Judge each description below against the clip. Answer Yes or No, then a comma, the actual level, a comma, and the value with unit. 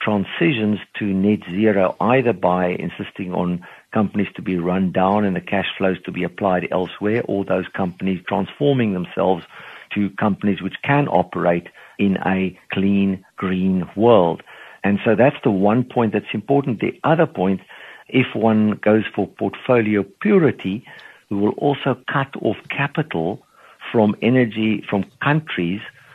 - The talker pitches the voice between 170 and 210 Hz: No, low, 100 Hz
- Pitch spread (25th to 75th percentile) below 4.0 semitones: Yes, average, 3.0 semitones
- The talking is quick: No, average, 145 wpm